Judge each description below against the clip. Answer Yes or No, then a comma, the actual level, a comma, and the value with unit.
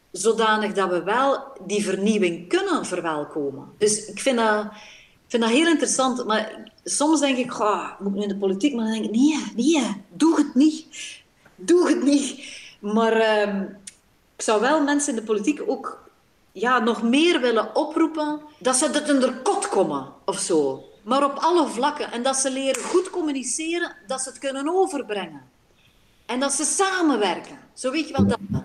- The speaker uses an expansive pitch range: Yes, wide, 6.1 semitones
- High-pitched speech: Yes, very high, 260 Hz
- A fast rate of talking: No, average, 180 wpm